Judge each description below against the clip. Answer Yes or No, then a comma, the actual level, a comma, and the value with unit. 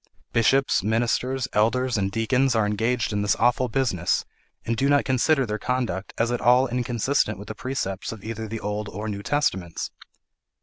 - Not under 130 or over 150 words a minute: No, average, 175 wpm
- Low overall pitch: Yes, low, 115 Hz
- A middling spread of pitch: Yes, average, 3.5 semitones